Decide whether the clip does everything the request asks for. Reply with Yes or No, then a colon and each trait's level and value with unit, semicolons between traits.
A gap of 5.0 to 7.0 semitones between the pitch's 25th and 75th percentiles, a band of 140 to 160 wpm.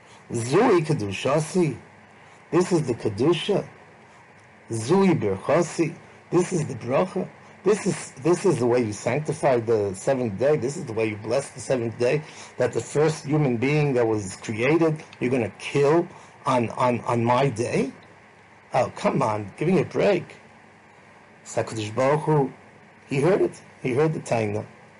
Yes: wide, 5.6 semitones; average, 150 wpm